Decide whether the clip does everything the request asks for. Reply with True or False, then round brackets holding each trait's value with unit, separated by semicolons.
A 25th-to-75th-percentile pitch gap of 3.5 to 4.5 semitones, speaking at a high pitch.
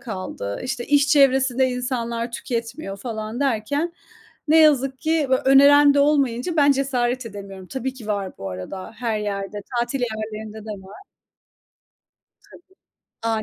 True (4.2 semitones; 245 Hz)